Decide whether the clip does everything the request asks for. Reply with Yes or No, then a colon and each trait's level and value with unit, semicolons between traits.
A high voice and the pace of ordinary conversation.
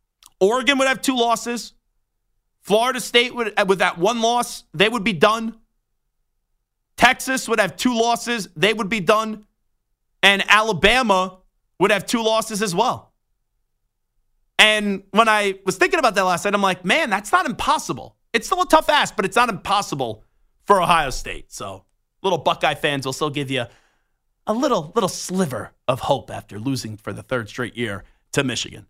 Yes: high, 200 Hz; average, 170 wpm